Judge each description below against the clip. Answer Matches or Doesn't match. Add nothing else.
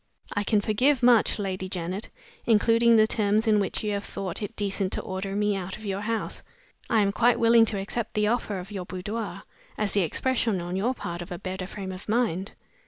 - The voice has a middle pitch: Doesn't match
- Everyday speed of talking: Doesn't match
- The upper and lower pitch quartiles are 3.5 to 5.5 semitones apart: Doesn't match